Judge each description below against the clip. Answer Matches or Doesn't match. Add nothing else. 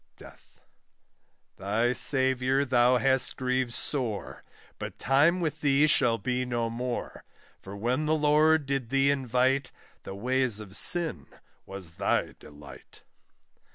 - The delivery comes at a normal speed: Doesn't match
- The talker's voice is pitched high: Doesn't match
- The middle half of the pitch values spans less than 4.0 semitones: Matches